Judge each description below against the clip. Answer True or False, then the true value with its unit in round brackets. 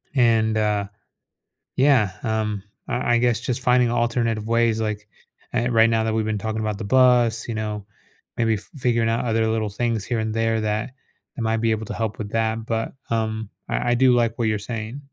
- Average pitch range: False (1.3 semitones)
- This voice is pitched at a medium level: False (115 Hz)